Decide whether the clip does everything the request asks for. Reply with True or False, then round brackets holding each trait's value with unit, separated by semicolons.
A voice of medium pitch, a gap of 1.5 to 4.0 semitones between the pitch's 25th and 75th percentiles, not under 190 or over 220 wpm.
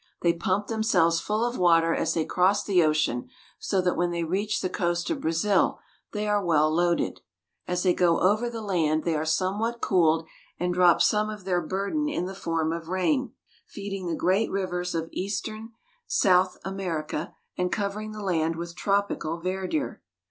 False (180 Hz; 3.4 semitones; 175 wpm)